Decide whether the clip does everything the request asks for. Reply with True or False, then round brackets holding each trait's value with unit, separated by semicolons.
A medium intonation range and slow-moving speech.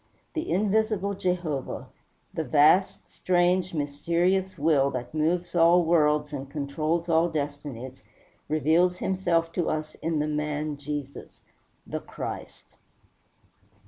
True (3.2 semitones; 110 wpm)